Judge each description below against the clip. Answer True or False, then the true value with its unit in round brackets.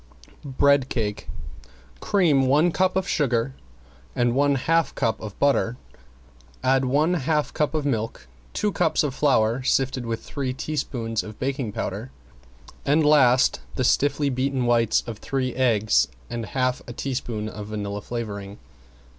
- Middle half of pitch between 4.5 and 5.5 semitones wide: False (3.9 semitones)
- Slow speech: False (145 wpm)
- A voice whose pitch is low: True (130 Hz)